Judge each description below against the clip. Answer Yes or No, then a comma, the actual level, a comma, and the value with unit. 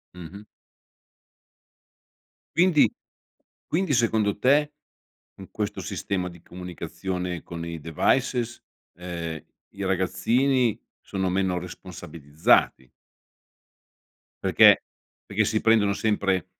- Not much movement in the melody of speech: No, average, 4.3 semitones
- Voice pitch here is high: No, very low, 95 Hz